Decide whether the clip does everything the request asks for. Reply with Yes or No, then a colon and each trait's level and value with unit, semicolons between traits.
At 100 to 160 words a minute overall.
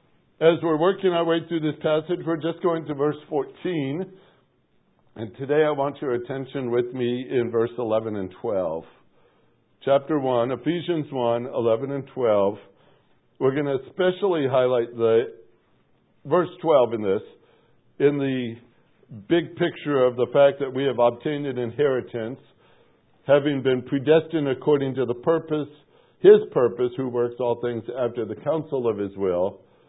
Yes: average, 155 wpm